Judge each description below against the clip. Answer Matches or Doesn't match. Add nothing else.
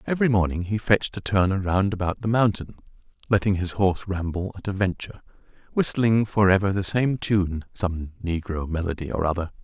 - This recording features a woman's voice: Doesn't match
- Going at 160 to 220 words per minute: Matches